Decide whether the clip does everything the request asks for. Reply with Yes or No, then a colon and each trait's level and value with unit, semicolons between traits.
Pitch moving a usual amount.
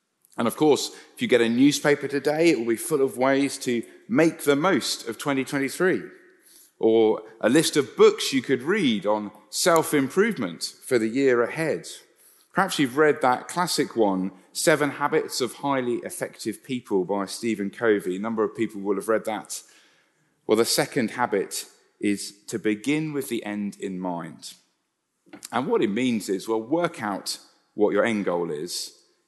No: wide, 6.9 semitones